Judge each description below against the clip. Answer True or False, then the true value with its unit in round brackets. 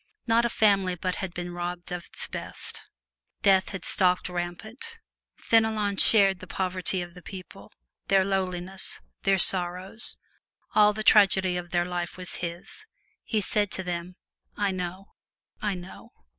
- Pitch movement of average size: False (2.3 semitones)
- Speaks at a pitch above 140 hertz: True (185 Hz)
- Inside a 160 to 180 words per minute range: False (150 wpm)